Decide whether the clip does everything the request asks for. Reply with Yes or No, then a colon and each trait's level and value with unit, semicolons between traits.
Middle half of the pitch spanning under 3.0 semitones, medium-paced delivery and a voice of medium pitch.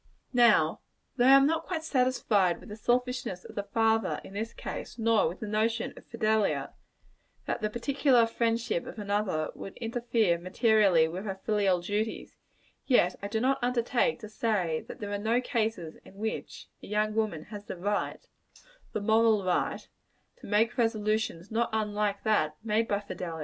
No: narrow, 2.4 semitones; average, 170 wpm; high, 215 Hz